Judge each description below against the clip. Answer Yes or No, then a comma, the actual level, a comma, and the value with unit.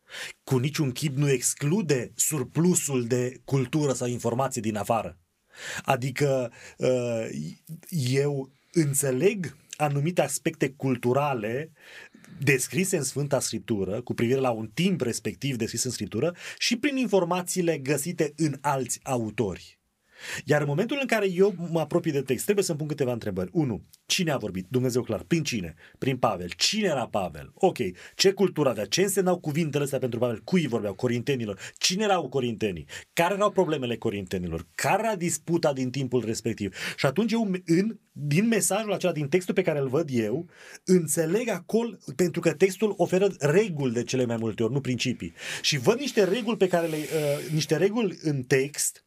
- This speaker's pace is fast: No, average, 160 wpm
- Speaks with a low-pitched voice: No, medium, 145 Hz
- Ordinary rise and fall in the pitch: No, wide, 6.3 semitones